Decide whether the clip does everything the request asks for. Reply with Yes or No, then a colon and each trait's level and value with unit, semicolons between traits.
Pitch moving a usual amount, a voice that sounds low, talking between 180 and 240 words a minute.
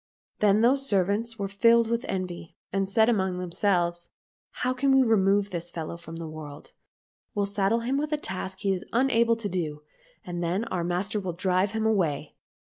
No: average, 4.4 semitones; high, 195 Hz; average, 190 wpm